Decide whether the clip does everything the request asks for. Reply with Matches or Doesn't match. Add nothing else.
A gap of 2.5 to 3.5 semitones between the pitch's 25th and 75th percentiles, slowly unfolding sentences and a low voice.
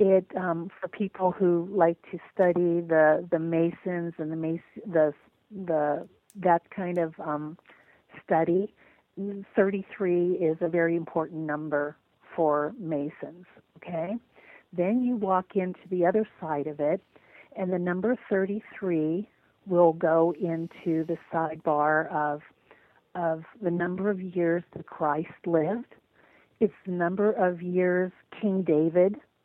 Doesn't match